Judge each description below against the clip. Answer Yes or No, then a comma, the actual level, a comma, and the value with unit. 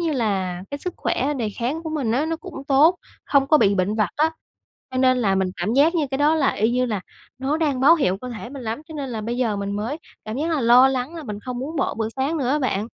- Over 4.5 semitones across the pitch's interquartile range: Yes, average, 5.1 semitones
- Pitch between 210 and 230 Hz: No, very high, 260 Hz